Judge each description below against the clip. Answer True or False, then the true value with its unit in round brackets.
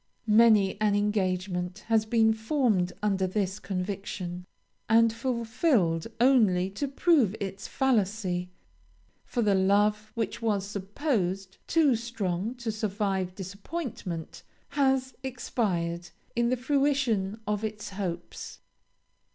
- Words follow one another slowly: True (110 wpm)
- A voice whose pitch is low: False (210 Hz)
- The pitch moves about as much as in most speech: True (3.7 semitones)